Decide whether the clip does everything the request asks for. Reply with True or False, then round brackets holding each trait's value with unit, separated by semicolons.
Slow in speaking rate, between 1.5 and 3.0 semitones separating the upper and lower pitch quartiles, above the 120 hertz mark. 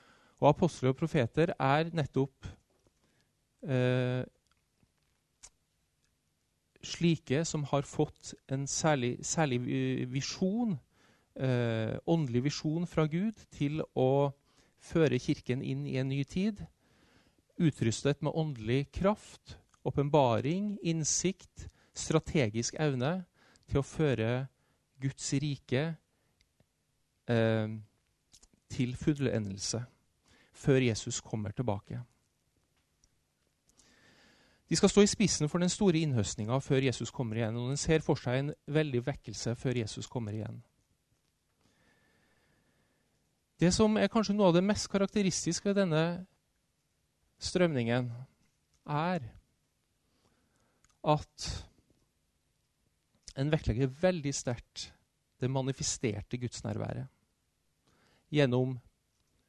False (85 wpm; 4.7 semitones; 135 Hz)